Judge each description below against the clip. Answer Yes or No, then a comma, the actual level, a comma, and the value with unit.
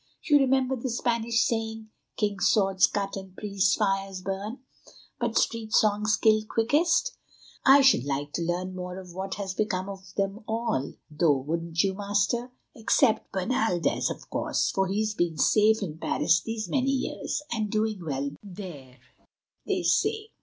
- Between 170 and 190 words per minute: No, average, 155 wpm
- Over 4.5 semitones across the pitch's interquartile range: No, average, 3.5 semitones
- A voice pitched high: Yes, high, 205 Hz